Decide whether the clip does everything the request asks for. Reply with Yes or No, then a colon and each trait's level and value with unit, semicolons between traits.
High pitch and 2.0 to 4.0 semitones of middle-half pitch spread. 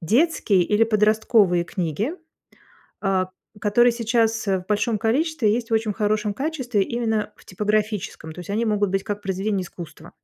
Yes: high, 210 Hz; average, 2.7 semitones